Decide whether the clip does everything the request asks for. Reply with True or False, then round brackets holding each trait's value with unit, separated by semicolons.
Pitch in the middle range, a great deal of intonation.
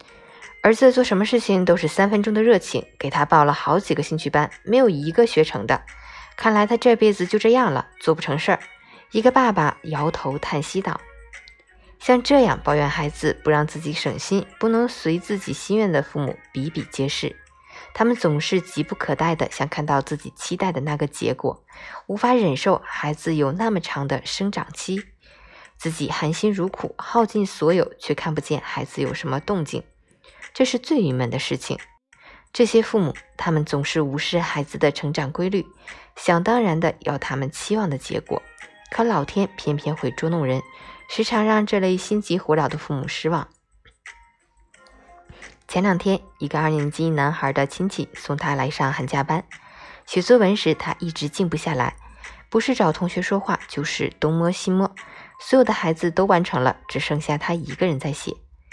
True (170 Hz; 5.9 semitones)